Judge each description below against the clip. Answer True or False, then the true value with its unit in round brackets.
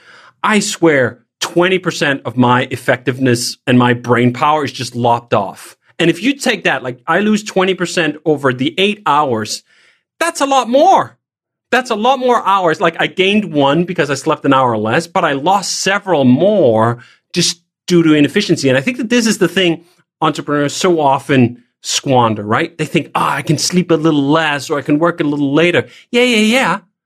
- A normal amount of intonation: False (5.7 semitones)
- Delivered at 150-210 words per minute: True (195 wpm)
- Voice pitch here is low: False (165 Hz)